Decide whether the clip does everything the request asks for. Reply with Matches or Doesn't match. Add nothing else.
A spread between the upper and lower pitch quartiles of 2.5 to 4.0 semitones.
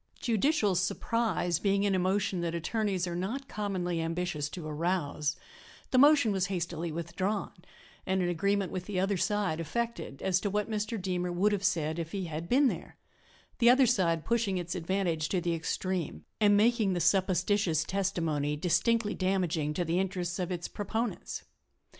Matches